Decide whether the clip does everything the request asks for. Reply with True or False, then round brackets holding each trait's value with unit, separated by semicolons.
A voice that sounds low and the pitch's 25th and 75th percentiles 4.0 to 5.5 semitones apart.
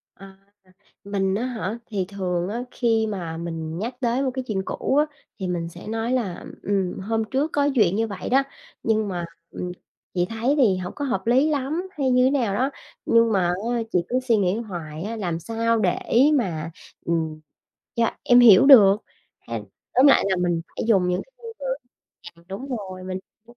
False (215 Hz; 5.1 semitones)